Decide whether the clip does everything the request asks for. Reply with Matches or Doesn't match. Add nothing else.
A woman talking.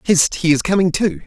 Doesn't match